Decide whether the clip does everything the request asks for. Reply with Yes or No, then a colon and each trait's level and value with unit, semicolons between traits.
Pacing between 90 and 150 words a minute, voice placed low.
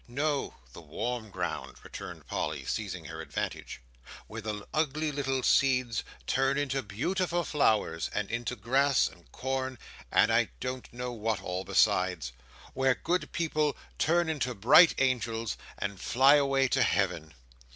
Yes: average, 140 wpm; low, 125 Hz